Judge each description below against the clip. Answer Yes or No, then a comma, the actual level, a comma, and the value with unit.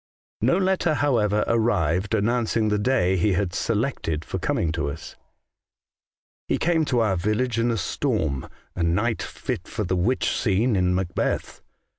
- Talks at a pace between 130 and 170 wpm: Yes, average, 165 wpm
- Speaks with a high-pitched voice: No, low, 105 Hz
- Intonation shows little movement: No, average, 4.9 semitones